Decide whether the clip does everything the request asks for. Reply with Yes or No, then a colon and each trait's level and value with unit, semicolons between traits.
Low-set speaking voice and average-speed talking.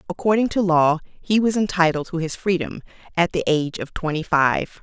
No: medium, 175 Hz; average, 185 wpm